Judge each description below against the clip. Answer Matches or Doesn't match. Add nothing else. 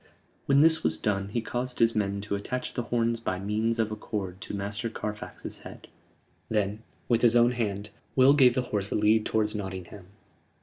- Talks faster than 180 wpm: Matches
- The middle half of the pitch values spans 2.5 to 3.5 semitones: Matches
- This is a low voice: Matches